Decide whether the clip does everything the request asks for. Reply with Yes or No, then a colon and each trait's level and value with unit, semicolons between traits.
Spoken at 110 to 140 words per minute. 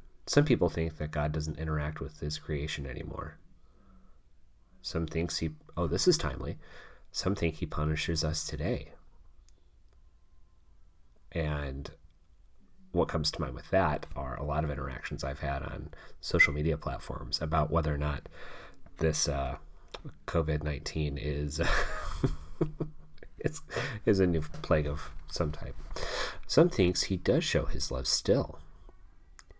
Yes: slow, 135 wpm